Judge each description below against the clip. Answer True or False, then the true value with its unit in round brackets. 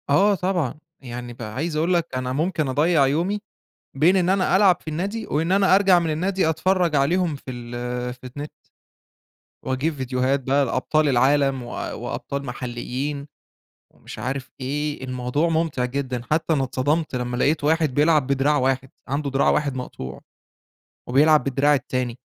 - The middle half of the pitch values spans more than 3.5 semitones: True (4.1 semitones)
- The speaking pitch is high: False (140 Hz)